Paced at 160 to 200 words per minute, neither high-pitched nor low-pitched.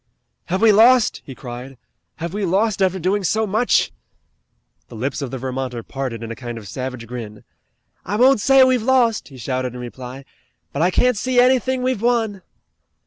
Yes: average, 185 wpm; medium, 180 Hz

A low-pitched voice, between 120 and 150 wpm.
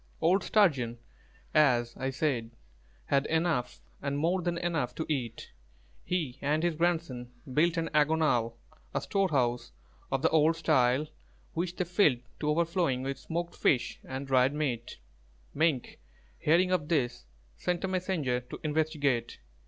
No: medium, 150 Hz; average, 140 wpm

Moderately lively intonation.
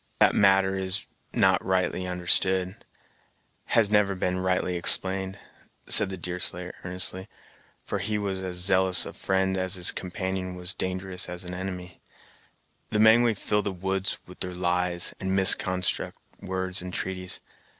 No: narrow, 0.9 semitones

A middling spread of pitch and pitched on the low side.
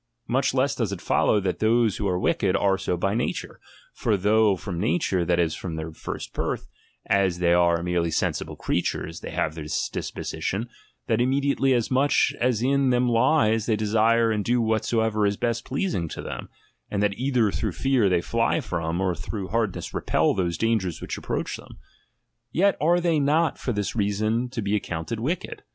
Yes: average, 4.8 semitones; low, 110 Hz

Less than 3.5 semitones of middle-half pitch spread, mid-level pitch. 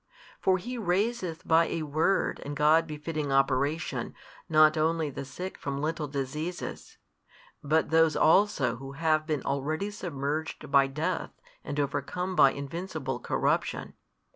Yes: average, 2.9 semitones; medium, 155 Hz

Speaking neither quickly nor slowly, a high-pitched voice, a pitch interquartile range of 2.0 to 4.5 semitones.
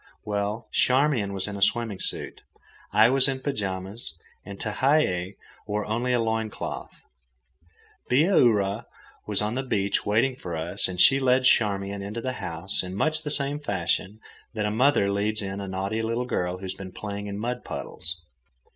No: average, 175 wpm; low, 105 Hz; average, 4.2 semitones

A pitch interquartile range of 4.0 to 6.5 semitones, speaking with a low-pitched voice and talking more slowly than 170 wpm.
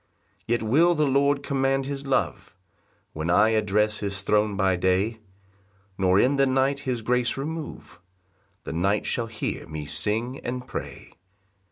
Yes: wide, 5.4 semitones; low, 115 Hz; average, 155 wpm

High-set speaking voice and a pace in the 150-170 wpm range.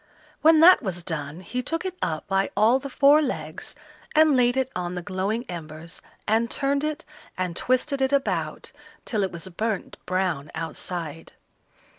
Yes: high, 215 Hz; average, 165 wpm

